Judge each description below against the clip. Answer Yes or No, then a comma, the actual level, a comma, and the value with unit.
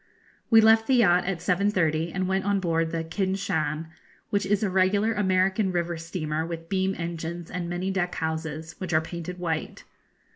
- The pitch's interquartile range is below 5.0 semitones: Yes, average, 2.8 semitones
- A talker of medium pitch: Yes, medium, 180 Hz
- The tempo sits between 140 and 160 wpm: No, average, 180 wpm